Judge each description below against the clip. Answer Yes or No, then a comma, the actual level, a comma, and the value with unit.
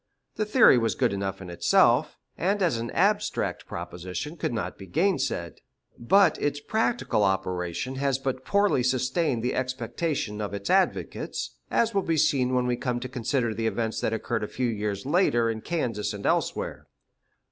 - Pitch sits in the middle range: No, low, 125 Hz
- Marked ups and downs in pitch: Yes, wide, 6.8 semitones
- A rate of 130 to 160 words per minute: No, average, 170 wpm